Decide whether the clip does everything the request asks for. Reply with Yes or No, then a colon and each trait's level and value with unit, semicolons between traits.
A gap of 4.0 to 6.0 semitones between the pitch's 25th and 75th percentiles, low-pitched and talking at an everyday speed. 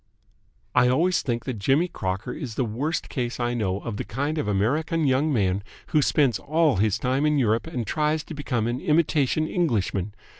Yes: wide, 5.5 semitones; low, 130 Hz; average, 195 wpm